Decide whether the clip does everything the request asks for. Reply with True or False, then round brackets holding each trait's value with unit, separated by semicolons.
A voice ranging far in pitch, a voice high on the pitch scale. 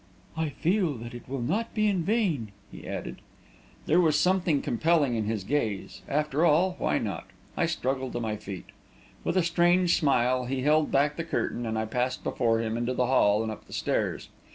False (5.9 semitones; 135 Hz)